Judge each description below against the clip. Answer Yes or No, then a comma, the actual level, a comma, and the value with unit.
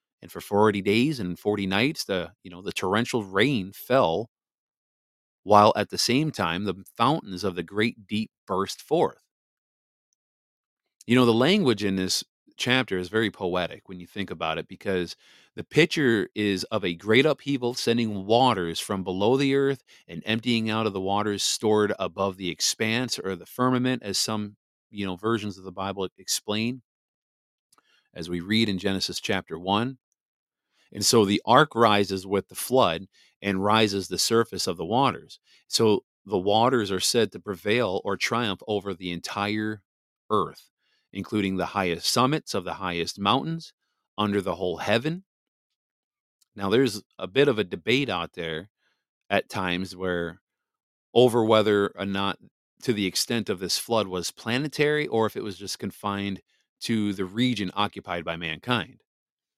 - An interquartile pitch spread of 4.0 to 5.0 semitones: No, average, 3.5 semitones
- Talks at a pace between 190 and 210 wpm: No, average, 160 wpm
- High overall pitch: No, low, 100 Hz